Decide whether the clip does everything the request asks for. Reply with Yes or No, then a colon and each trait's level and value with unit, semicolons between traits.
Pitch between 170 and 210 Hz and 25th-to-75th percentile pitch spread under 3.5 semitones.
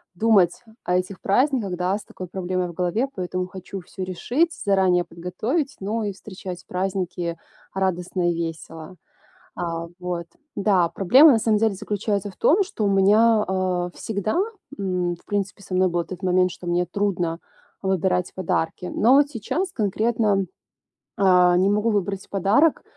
Yes: high, 190 Hz; average, 2.8 semitones